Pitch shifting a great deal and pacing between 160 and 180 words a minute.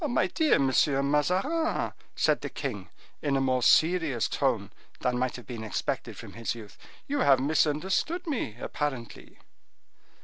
No: wide, 6.6 semitones; average, 145 wpm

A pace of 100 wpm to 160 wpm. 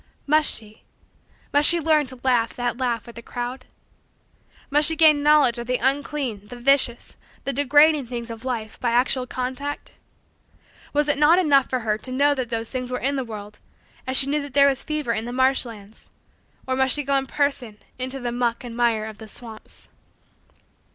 No: average, 200 wpm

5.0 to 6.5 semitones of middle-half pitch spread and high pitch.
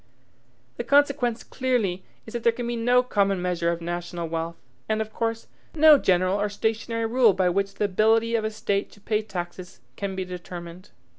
No: average, 4.1 semitones; high, 205 Hz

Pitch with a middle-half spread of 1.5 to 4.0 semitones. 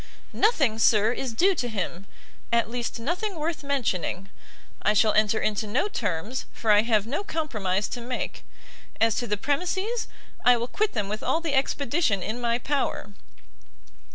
No: wide, 5.6 semitones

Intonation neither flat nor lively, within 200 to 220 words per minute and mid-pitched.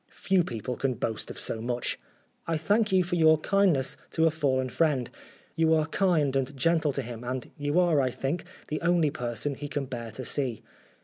Yes: average, 4.2 semitones; fast, 205 wpm; medium, 145 Hz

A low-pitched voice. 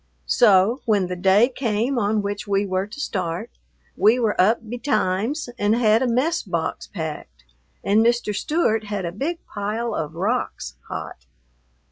No: high, 210 Hz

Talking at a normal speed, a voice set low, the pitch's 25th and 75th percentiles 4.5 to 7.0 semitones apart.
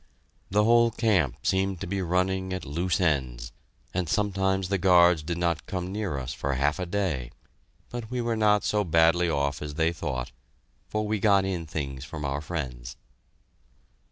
Yes: average, 175 wpm; very low, 90 Hz; average, 4.9 semitones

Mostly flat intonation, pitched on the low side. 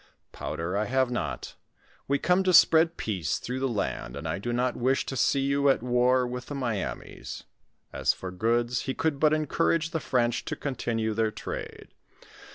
No: average, 3.7 semitones; low, 125 Hz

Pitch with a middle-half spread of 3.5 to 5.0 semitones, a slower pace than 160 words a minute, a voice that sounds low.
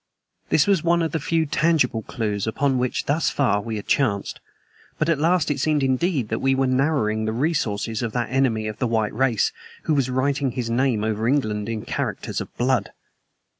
No: average, 4.6 semitones; average, 200 wpm; low, 130 Hz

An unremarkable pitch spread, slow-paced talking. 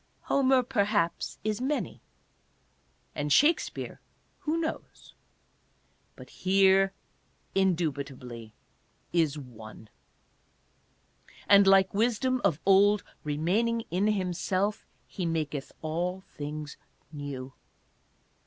No: wide, 5.9 semitones; slow, 95 wpm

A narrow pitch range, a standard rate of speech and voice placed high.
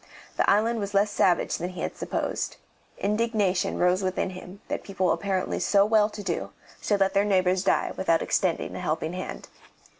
Yes: narrow, 2.0 semitones; average, 180 wpm; high, 195 Hz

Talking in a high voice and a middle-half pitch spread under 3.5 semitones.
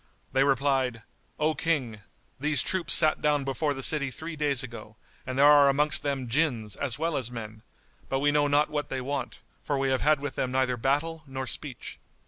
No: medium, 140 Hz; narrow, 2.5 semitones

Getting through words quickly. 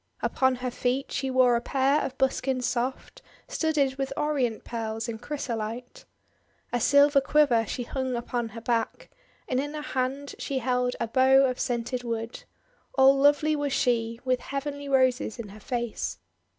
No: average, 165 wpm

